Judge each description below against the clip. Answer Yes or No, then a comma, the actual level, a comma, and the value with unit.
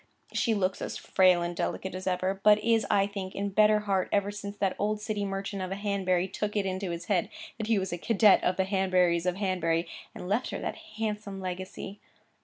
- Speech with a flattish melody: Yes, narrow, 1.9 semitones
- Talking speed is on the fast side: Yes, fast, 215 wpm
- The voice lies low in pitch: No, high, 195 Hz